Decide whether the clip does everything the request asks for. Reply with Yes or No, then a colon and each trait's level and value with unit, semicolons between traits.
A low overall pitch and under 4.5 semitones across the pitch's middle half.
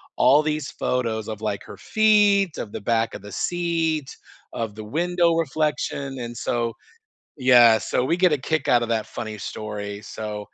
No: low, 125 Hz; wide, 6.6 semitones